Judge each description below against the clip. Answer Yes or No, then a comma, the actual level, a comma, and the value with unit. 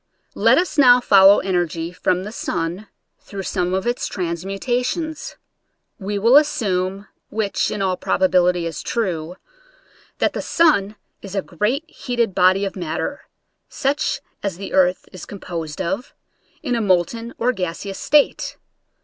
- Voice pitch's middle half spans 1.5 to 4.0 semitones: No, average, 4.6 semitones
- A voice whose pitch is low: No, high, 195 Hz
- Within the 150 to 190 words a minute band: No, average, 140 wpm